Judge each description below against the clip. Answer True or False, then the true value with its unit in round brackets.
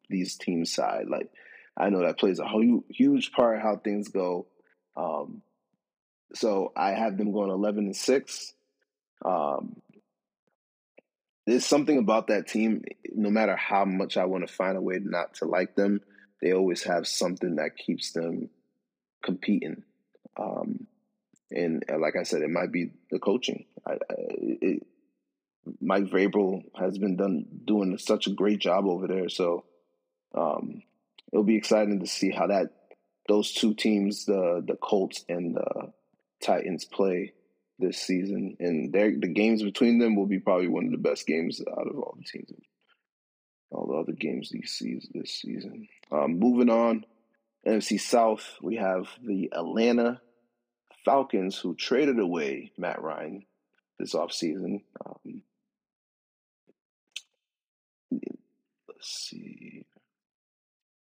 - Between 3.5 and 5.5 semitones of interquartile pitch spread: True (3.9 semitones)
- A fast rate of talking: False (140 wpm)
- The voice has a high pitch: False (105 Hz)